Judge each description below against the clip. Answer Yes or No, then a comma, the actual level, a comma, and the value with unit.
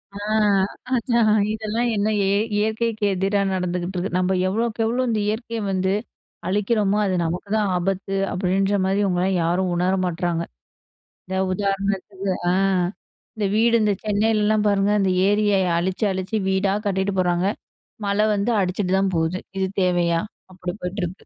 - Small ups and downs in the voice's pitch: Yes, narrow, 2.3 semitones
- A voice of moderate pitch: No, high, 195 Hz